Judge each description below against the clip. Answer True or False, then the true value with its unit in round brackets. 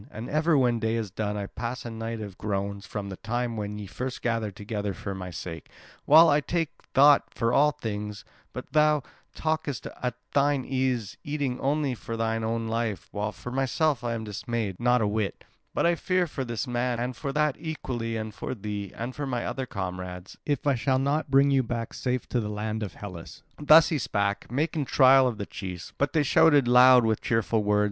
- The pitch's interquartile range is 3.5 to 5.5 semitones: True (4.6 semitones)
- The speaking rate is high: True (210 wpm)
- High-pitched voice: False (120 Hz)